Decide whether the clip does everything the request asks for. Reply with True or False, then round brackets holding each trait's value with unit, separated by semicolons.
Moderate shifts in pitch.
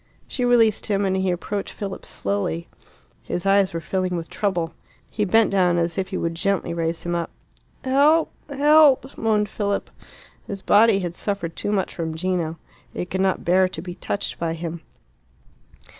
True (3.5 semitones)